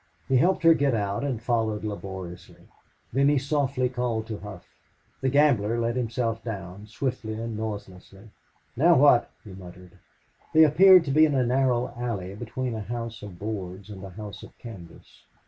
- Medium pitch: No, low, 115 Hz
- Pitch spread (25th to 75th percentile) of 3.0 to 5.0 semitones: Yes, average, 4.4 semitones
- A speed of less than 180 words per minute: Yes, average, 170 wpm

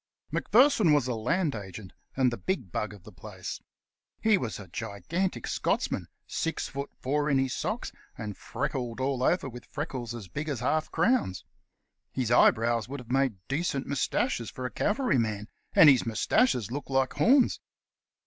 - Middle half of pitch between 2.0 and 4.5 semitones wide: No, average, 5.1 semitones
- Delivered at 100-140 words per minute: No, average, 165 wpm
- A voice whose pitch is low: Yes, low, 130 Hz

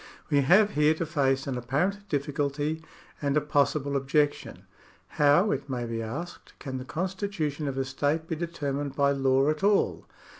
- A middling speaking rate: Yes, average, 165 wpm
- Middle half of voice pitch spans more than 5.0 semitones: No, average, 2.8 semitones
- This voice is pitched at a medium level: Yes, medium, 145 Hz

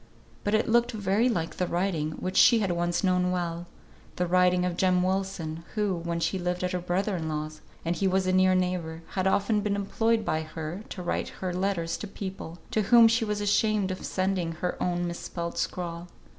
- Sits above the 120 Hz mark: Yes, medium, 185 Hz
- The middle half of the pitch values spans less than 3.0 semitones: Yes, narrow, 2.5 semitones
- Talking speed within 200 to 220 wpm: Yes, fast, 205 wpm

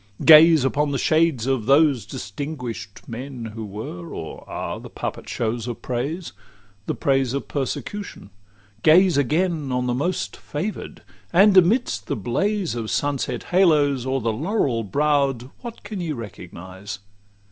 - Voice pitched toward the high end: No, low, 135 Hz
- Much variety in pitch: Yes, wide, 5.8 semitones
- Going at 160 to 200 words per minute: No, average, 145 wpm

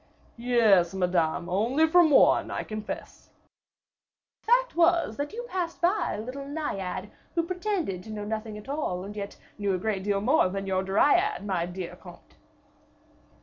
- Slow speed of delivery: No, average, 165 wpm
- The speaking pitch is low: No, high, 215 Hz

